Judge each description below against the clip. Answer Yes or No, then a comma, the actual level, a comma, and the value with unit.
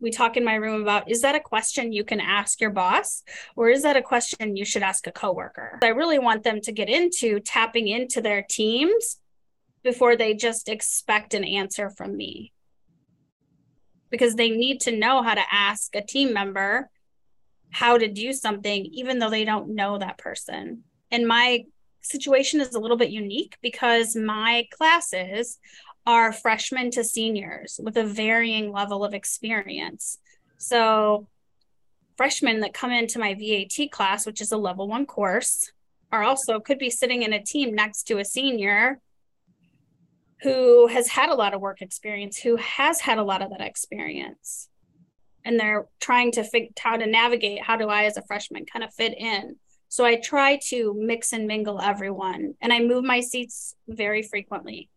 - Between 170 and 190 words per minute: Yes, average, 175 wpm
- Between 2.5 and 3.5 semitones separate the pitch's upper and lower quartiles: Yes, average, 2.8 semitones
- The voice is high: Yes, high, 230 Hz